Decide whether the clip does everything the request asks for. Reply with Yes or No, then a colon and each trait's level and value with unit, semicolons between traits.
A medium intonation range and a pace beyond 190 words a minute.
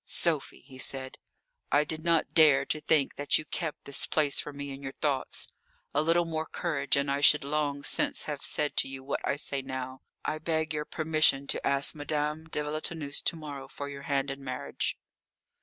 No: narrow, 2.0 semitones; average, 200 wpm